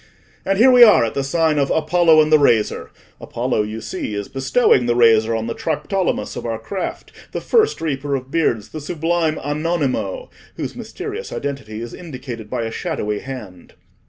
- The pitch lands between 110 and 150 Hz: Yes, medium, 140 Hz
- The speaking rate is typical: Yes, average, 180 wpm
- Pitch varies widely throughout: Yes, wide, 6.3 semitones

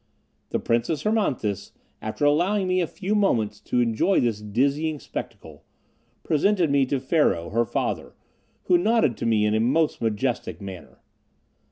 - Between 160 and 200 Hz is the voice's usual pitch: No, low, 135 Hz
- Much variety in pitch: Yes, wide, 7.8 semitones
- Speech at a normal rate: Yes, average, 150 wpm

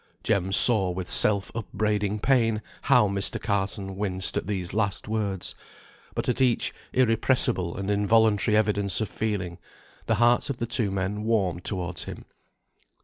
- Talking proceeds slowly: No, average, 145 wpm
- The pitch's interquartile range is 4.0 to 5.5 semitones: No, narrow, 2.5 semitones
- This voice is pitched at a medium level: No, low, 105 Hz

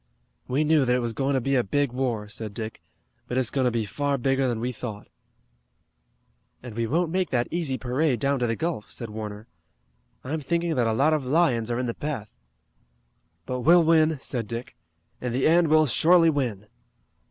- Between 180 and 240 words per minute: Yes, average, 200 wpm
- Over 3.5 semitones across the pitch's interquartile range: Yes, average, 4.6 semitones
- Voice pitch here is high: No, low, 130 Hz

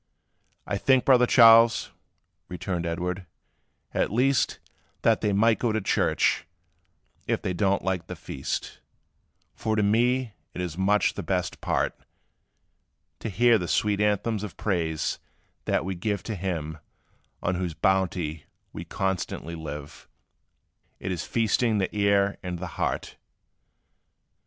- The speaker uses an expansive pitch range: No, average, 3.7 semitones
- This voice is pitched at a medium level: No, low, 100 Hz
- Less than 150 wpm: Yes, slow, 135 wpm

